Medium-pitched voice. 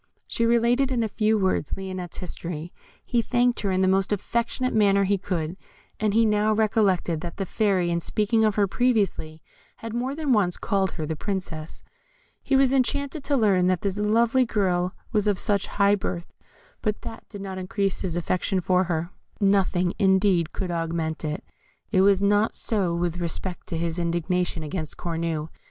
No: high, 195 Hz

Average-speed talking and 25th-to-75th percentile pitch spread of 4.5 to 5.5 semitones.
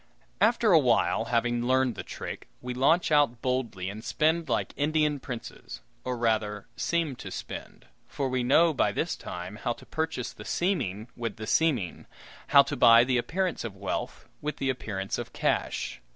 Yes: average, 170 wpm; average, 5.1 semitones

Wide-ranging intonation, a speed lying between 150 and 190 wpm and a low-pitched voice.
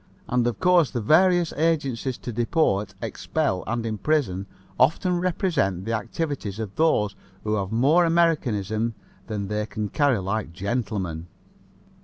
No: wide, 7.3 semitones; slow, 135 wpm; low, 115 Hz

